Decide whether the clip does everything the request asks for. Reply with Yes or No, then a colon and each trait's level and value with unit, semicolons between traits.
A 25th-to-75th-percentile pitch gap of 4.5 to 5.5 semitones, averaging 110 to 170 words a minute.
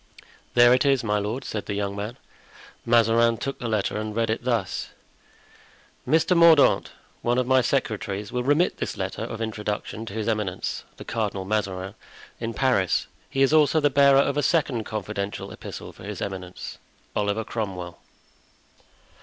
No: average, 4.1 semitones; average, 160 wpm